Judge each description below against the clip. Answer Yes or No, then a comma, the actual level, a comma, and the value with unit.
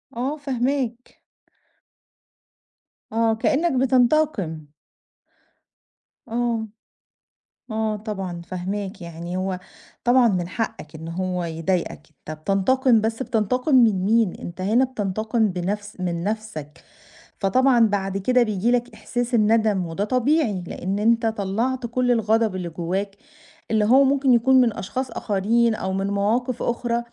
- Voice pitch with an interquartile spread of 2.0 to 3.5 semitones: No, average, 4.3 semitones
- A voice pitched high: Yes, high, 220 Hz